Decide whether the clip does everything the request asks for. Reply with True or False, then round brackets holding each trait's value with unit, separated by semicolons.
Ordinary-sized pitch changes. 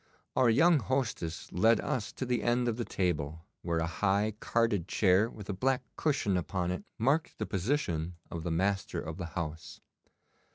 False (5.8 semitones)